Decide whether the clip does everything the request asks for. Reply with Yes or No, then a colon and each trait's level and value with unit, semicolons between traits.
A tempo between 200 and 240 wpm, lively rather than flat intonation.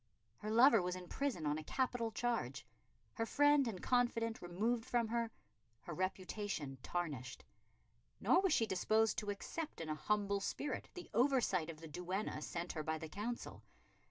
No: average, 165 wpm; wide, 5.8 semitones